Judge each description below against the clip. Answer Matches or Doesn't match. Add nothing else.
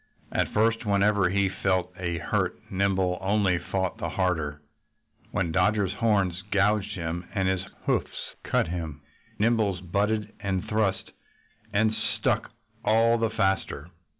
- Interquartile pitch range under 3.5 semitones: Matches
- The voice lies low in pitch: Matches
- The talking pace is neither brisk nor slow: Doesn't match